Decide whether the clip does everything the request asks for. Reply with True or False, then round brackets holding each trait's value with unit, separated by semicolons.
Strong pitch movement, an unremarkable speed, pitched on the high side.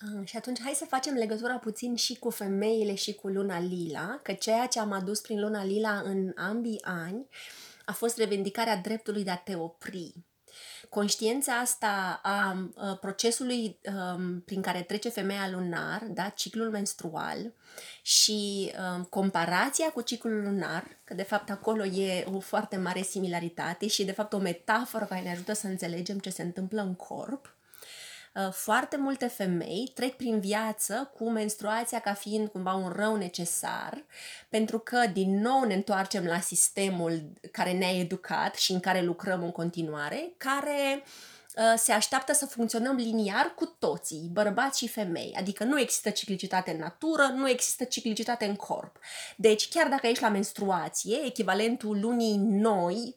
False (3.5 semitones; 155 wpm; 210 Hz)